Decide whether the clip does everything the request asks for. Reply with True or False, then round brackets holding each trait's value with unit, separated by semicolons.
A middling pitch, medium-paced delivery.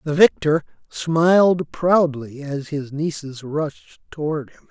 False (155 Hz; 130 wpm)